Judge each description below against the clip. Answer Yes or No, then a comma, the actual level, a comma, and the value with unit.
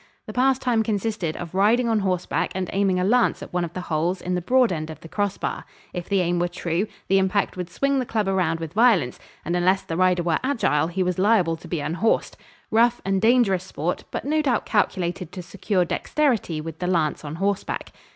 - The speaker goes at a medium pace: No, fast, 215 wpm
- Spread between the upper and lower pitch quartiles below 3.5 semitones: No, average, 4.1 semitones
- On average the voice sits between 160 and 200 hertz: Yes, medium, 185 Hz